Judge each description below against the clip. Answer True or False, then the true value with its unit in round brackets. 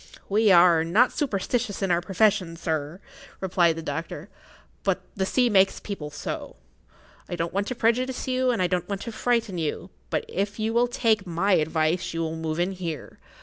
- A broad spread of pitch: False (4.8 semitones)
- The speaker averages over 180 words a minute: True (190 wpm)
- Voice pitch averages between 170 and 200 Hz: True (190 Hz)